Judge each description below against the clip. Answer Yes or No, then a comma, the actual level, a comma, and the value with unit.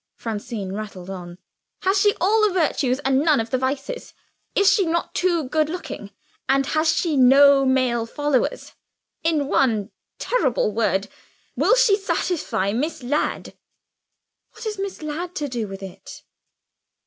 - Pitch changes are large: Yes, wide, 6.9 semitones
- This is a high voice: Yes, very high, 280 Hz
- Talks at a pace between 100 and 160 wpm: Yes, average, 150 wpm